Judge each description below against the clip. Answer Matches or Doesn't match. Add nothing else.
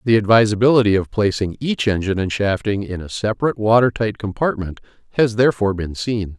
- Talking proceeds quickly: Doesn't match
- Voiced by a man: Matches